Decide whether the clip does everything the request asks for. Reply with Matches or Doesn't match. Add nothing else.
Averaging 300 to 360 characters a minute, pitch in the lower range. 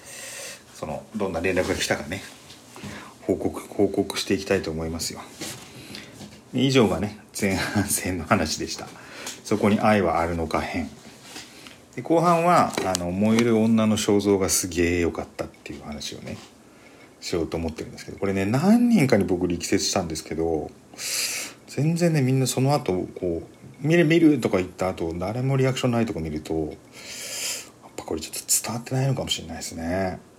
Matches